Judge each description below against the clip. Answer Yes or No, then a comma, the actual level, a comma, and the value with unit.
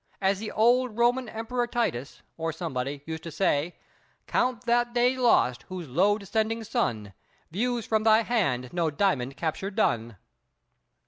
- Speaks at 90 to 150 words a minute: Yes, average, 145 wpm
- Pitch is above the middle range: Yes, high, 200 Hz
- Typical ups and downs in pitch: No, wide, 7.6 semitones